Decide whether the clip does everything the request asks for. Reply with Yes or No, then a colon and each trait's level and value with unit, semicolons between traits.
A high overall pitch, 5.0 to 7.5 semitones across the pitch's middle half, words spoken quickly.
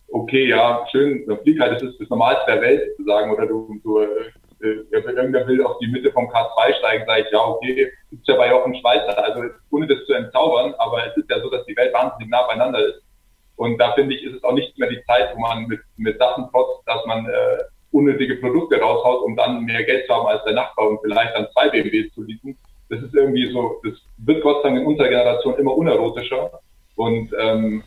No: low, 125 Hz; wide, 5.5 semitones; fast, 225 wpm